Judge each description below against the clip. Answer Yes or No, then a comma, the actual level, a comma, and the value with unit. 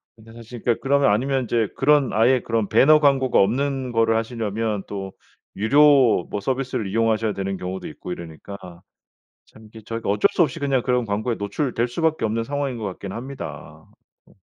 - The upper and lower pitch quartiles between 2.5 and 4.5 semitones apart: Yes, average, 4.1 semitones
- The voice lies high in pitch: No, low, 115 Hz